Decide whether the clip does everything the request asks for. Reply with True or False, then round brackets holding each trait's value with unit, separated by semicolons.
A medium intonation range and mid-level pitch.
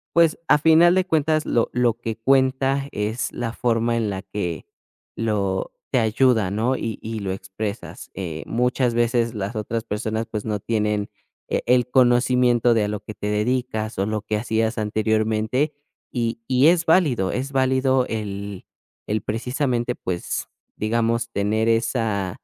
False (3.0 semitones; 115 Hz)